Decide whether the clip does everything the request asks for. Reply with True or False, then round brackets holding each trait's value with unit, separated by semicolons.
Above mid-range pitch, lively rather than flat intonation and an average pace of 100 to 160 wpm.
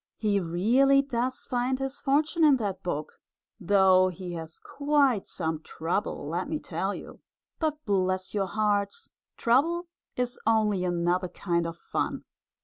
True (205 Hz; 6.9 semitones; 140 wpm)